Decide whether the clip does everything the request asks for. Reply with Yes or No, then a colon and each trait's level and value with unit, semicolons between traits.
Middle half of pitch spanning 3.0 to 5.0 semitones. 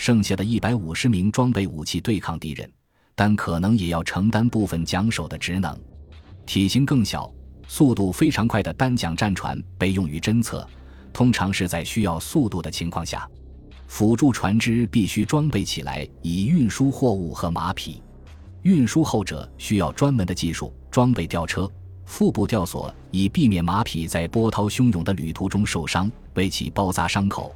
No: wide, 5.4 semitones